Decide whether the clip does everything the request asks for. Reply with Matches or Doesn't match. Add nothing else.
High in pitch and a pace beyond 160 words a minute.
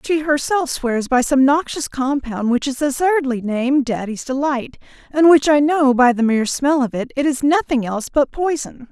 Matches